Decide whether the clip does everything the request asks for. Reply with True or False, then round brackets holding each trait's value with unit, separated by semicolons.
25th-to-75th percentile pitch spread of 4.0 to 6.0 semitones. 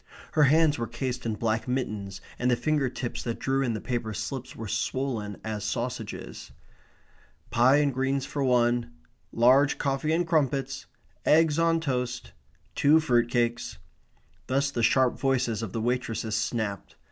False (3.1 semitones)